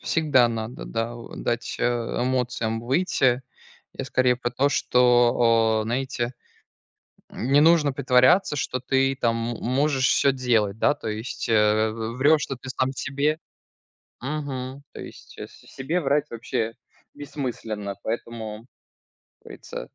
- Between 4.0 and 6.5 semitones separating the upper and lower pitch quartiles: No, average, 2.8 semitones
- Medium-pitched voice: No, low, 125 Hz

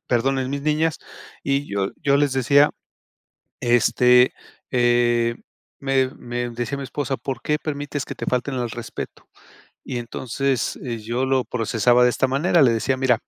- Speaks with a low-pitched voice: Yes, low, 130 Hz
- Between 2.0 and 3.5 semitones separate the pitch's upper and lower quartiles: Yes, narrow, 2.4 semitones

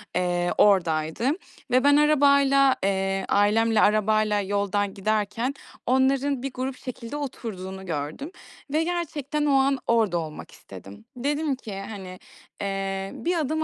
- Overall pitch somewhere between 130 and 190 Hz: No, high, 220 Hz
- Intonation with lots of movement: Yes, wide, 6.1 semitones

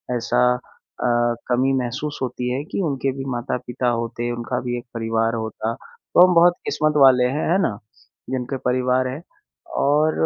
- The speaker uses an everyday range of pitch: No, narrow, 2.2 semitones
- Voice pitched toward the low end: Yes, low, 125 Hz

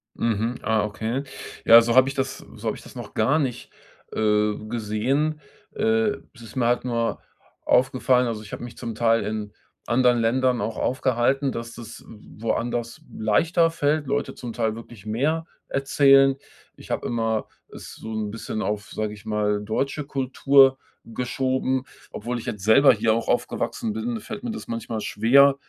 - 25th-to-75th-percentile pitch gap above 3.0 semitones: Yes, average, 3.5 semitones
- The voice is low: Yes, low, 120 Hz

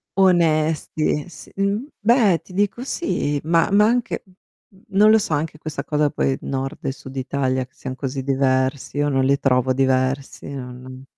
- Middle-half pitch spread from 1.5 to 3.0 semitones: No, wide, 5.7 semitones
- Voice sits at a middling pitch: Yes, medium, 145 Hz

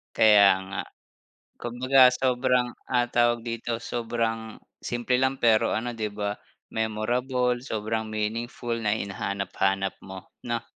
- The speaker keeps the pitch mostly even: Yes, narrow, 2.1 semitones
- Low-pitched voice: Yes, low, 115 Hz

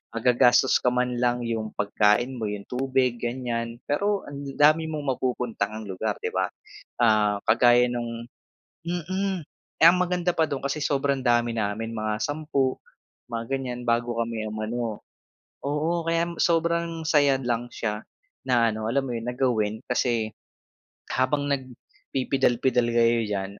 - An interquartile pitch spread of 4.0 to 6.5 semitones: No, average, 3.6 semitones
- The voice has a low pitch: Yes, low, 125 Hz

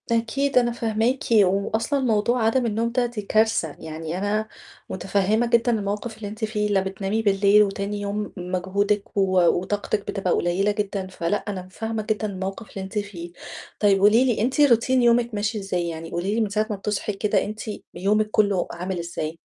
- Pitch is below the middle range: No, high, 205 Hz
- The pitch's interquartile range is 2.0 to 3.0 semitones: Yes, narrow, 2.5 semitones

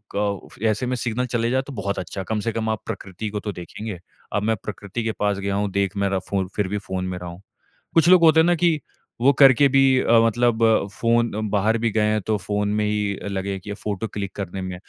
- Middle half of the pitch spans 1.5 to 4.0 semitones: Yes, average, 2.8 semitones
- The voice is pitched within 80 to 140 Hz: Yes, low, 105 Hz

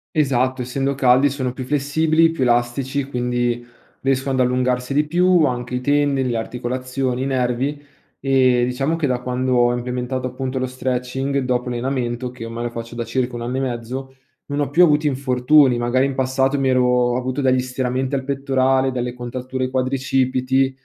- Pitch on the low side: Yes, low, 130 Hz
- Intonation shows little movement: Yes, narrow, 1.5 semitones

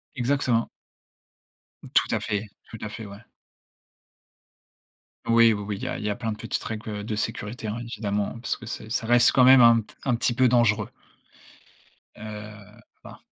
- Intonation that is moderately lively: No, narrow, 2.1 semitones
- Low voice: Yes, low, 110 Hz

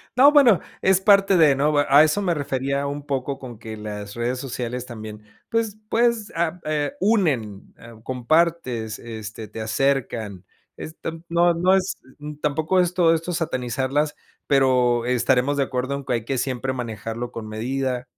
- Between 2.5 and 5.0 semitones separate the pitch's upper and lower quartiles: No, wide, 5.5 semitones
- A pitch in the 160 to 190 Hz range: No, low, 135 Hz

